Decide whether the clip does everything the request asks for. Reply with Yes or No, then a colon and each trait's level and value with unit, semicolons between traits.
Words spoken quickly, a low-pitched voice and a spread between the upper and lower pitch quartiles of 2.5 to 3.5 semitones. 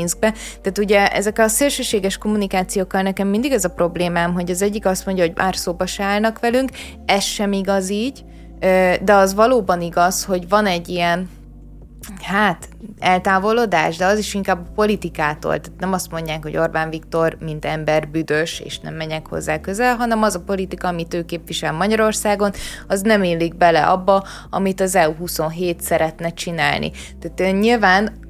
No: fast, 165 wpm; medium, 185 Hz; average, 3.1 semitones